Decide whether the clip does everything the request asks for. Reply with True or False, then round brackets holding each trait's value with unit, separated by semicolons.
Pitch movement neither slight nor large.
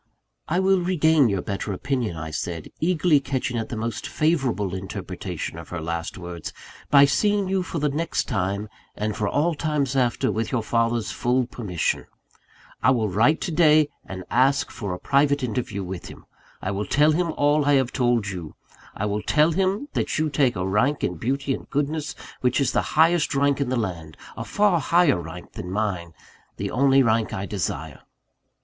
False (7.0 semitones)